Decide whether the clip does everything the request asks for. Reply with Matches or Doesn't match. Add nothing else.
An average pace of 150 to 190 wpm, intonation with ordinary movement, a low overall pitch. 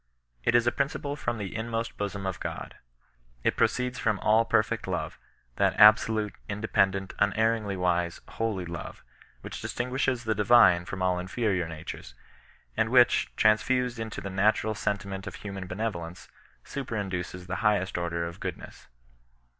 Matches